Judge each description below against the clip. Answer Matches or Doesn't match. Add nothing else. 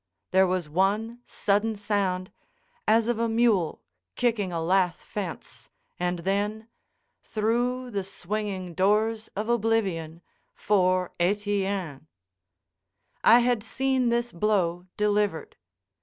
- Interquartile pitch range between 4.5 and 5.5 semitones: Doesn't match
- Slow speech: Matches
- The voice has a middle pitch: Doesn't match